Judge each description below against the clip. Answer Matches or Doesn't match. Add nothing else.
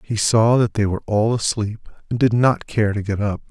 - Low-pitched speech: Matches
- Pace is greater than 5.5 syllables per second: Doesn't match